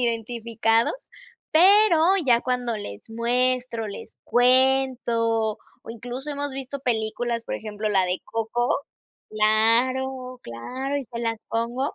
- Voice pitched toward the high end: Yes, high, 235 Hz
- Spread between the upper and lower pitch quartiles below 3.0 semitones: Yes, narrow, 2.4 semitones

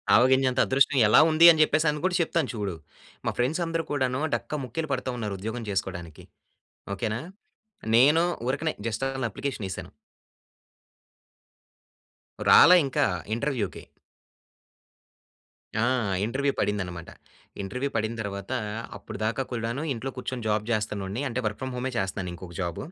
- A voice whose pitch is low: Yes, low, 120 Hz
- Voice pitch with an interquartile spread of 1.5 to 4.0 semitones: No, average, 4.8 semitones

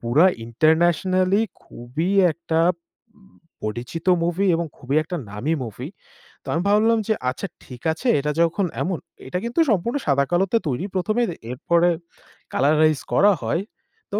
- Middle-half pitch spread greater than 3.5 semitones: Yes, wide, 5.4 semitones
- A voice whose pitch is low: No, medium, 170 Hz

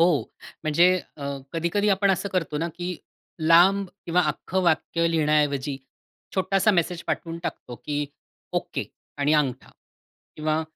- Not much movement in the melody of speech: No, average, 3.3 semitones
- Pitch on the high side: No, medium, 165 Hz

